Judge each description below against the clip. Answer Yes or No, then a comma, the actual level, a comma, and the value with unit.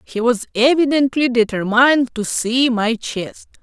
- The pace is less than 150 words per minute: Yes, slow, 135 wpm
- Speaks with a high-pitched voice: Yes, high, 245 Hz